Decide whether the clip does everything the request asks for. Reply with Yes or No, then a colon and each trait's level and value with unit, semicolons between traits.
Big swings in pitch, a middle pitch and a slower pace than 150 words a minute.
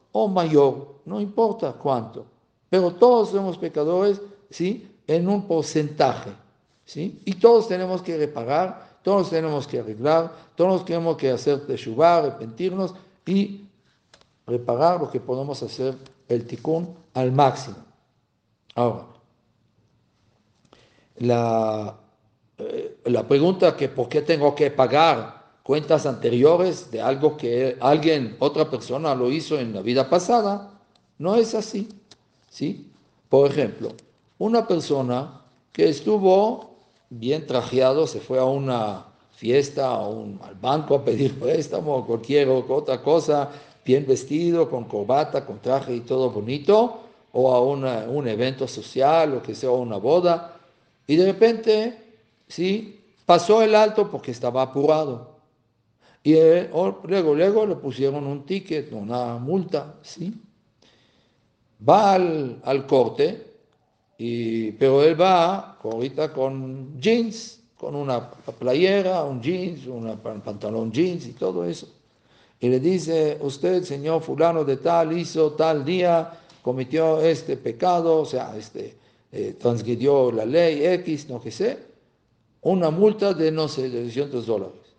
Yes: wide, 6.1 semitones; medium, 150 Hz; average, 135 wpm